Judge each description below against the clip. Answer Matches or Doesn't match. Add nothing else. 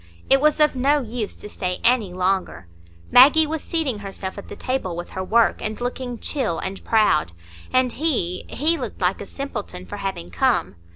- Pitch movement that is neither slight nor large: Doesn't match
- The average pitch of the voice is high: Matches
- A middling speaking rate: Matches